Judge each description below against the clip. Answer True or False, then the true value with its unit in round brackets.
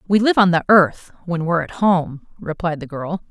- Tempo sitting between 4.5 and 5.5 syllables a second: True (5.0 syllables/s)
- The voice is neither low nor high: True (170 Hz)